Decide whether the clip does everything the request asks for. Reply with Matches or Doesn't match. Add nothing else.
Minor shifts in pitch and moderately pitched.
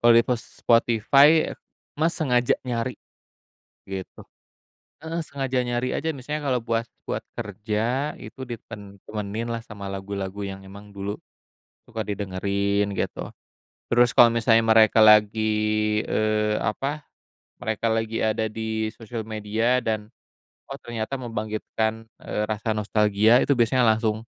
Doesn't match